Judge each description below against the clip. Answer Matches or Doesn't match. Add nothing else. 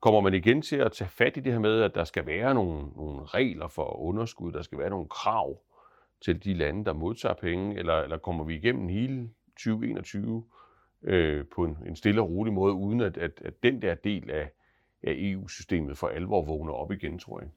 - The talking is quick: Doesn't match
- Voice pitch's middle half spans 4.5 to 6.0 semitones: Matches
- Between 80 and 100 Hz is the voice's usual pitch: Matches